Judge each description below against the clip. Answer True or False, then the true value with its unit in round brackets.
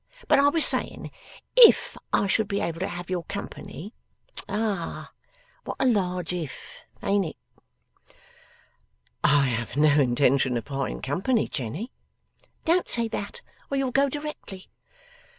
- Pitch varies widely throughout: True (8.2 semitones)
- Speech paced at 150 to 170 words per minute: False (135 wpm)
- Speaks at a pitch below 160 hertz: False (190 Hz)